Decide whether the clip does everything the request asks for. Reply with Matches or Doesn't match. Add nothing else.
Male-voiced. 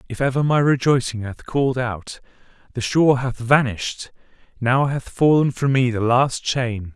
Matches